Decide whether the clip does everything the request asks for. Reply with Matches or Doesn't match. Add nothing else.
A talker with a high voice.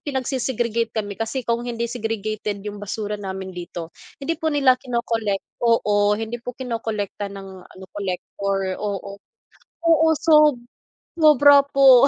Matches